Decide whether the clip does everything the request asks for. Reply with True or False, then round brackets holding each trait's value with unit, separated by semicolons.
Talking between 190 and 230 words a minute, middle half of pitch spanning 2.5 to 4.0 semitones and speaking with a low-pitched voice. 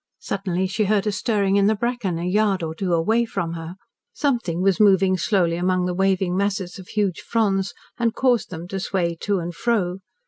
False (200 wpm; 2.9 semitones; 195 Hz)